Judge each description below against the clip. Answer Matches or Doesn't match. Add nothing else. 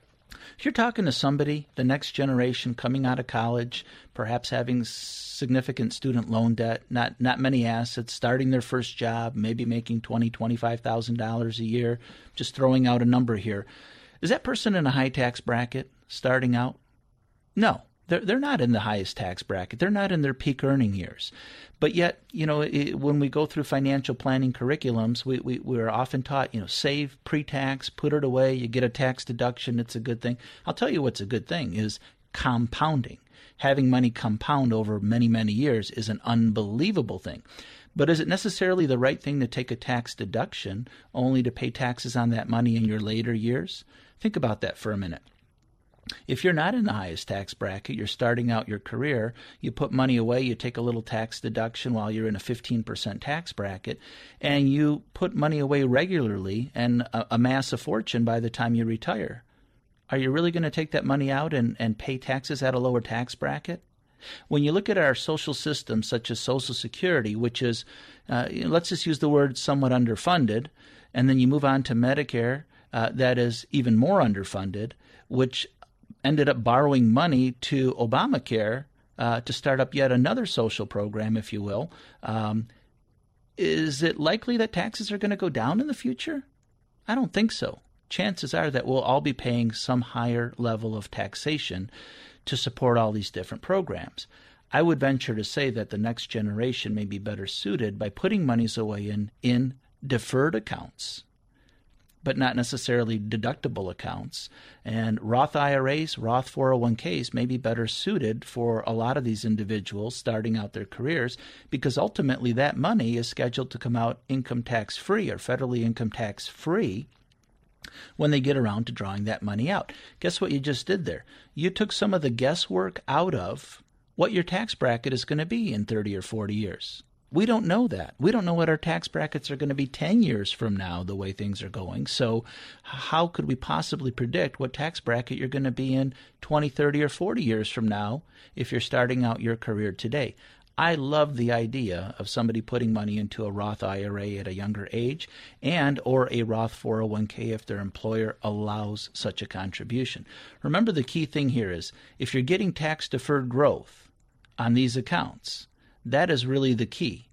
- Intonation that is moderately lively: Matches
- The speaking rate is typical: Matches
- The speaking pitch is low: Matches